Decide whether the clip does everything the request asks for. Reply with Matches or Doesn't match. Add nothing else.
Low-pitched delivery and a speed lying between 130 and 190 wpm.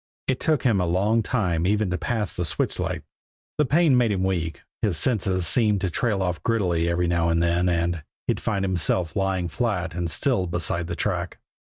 Doesn't match